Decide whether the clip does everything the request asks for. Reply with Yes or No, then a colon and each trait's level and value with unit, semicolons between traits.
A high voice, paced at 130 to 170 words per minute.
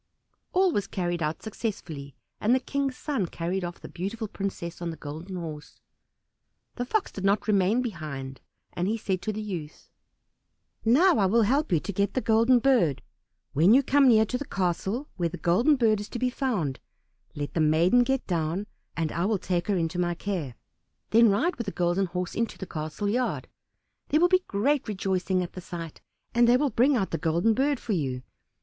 No: high, 200 Hz; average, 200 wpm